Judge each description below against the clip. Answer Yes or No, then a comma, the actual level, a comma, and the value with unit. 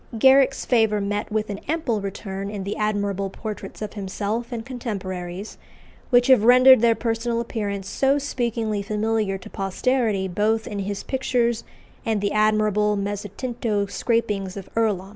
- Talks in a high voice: Yes, high, 215 Hz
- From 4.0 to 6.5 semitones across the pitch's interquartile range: No, average, 2.7 semitones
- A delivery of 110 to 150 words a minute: Yes, average, 145 wpm